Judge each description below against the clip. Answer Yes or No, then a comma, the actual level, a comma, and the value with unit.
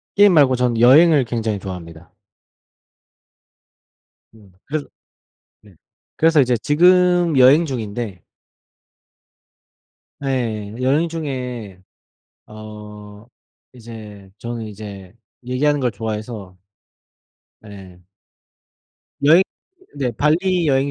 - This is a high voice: No, low, 120 Hz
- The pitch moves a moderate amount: No, wide, 5.7 semitones